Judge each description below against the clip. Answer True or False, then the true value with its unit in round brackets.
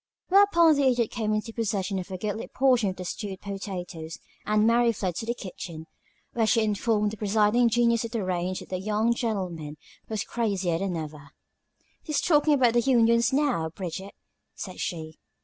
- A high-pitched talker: True (215 Hz)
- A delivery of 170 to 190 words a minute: True (180 wpm)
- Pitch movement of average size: True (4.1 semitones)